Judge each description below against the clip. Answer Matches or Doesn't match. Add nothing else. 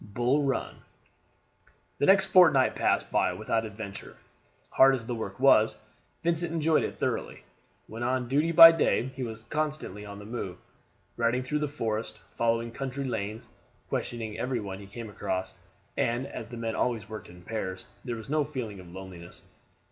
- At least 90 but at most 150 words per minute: Doesn't match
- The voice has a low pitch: Matches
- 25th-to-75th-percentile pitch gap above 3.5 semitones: Matches